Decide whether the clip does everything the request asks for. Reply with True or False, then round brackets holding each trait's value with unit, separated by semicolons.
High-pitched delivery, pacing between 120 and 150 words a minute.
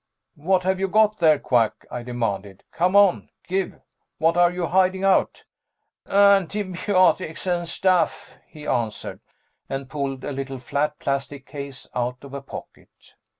False (155 Hz; 140 wpm)